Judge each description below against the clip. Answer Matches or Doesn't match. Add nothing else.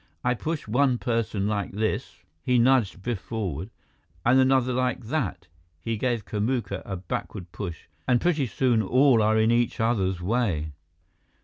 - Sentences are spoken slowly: Doesn't match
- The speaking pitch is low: Matches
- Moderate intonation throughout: Matches